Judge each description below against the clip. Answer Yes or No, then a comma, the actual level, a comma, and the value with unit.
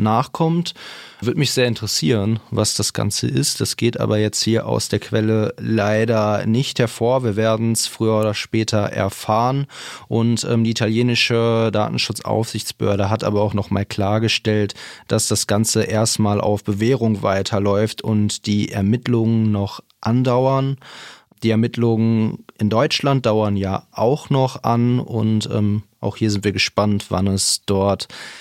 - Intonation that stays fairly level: Yes, narrow, 1.9 semitones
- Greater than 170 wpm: No, average, 145 wpm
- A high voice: No, low, 110 Hz